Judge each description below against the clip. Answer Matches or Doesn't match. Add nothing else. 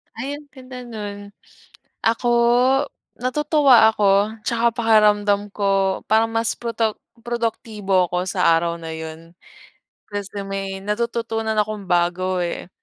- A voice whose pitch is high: Matches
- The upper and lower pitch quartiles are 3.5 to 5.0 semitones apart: Doesn't match